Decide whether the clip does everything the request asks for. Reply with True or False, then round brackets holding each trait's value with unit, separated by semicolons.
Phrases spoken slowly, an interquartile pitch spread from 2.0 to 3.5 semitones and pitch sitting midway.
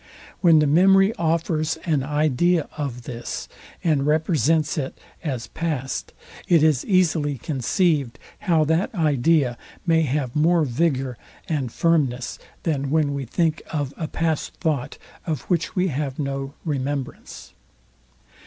True (130 wpm; 3.2 semitones; 150 Hz)